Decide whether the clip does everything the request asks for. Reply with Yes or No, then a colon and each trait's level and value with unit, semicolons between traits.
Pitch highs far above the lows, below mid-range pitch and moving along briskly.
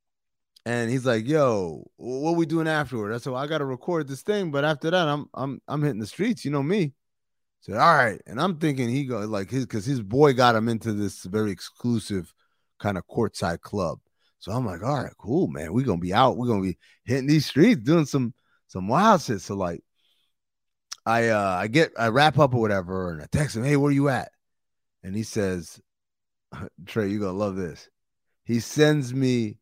Yes: wide, 5.8 semitones; low, 120 Hz; fast, 215 wpm